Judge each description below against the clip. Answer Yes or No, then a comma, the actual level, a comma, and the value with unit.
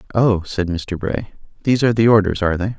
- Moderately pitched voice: No, low, 100 Hz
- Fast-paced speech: Yes, fast, 215 wpm